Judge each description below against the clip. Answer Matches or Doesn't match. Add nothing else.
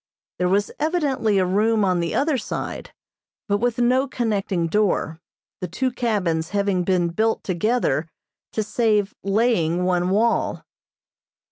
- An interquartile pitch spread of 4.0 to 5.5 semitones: Matches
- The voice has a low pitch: Doesn't match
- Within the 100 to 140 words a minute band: Matches